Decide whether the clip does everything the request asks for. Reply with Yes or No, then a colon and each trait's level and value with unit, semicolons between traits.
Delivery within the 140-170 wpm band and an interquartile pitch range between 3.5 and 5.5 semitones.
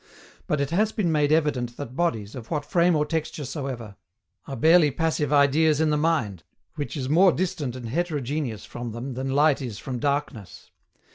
No: average, 185 wpm; average, 4.0 semitones